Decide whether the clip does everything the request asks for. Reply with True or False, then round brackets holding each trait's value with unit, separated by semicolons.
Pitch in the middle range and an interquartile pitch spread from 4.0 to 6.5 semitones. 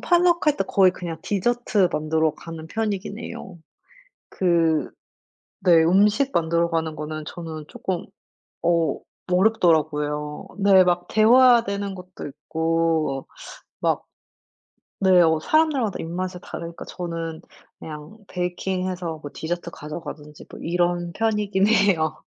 False (175 Hz; 3.6 semitones)